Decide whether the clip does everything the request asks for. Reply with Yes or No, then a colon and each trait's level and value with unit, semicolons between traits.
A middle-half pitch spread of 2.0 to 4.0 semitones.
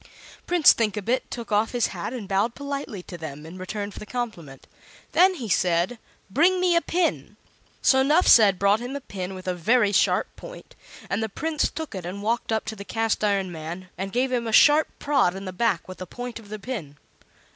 No: average, 5.3 semitones